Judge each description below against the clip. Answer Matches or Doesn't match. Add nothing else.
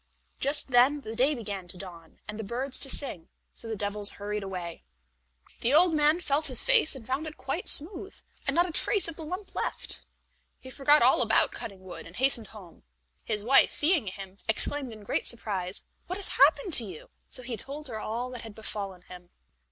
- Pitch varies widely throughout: Matches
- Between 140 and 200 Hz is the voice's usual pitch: Doesn't match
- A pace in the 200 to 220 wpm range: Matches